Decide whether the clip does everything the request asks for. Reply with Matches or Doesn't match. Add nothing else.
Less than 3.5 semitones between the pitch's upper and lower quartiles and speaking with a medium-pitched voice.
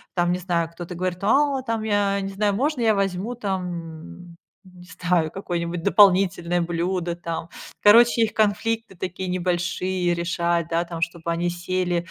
Matches